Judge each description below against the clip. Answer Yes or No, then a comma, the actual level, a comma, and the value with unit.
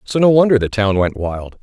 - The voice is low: Yes, low, 115 Hz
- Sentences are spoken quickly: Yes, fast, 260 wpm